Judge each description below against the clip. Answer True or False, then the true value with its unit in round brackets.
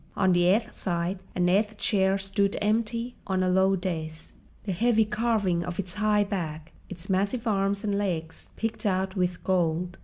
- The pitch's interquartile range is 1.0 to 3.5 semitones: True (2.8 semitones)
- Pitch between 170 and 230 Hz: True (190 Hz)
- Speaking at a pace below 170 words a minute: False (175 wpm)